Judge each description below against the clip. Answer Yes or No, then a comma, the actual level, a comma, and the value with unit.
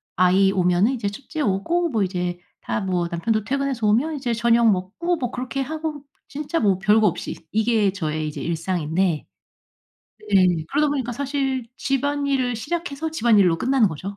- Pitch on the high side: Yes, high, 225 Hz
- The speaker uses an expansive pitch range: Yes, wide, 6.6 semitones